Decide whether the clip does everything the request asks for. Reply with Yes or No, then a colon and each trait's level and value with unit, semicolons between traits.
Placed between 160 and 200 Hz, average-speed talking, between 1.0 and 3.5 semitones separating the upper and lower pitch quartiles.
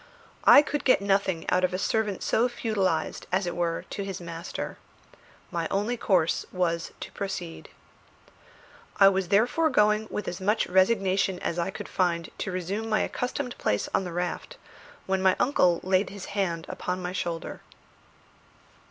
Yes: high, 190 Hz; average, 160 wpm; average, 2.9 semitones